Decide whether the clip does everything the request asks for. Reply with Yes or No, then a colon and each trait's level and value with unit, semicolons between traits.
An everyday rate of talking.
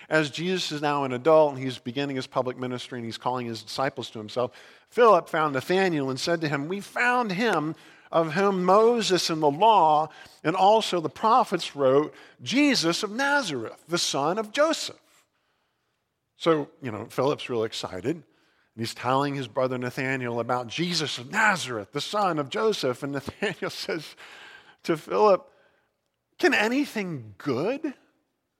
Yes: average, 155 wpm